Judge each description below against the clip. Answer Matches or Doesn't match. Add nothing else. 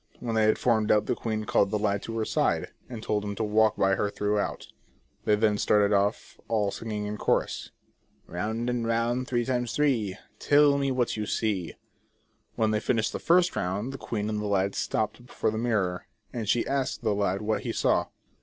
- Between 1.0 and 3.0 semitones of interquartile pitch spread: Matches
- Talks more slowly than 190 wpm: Doesn't match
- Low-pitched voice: Matches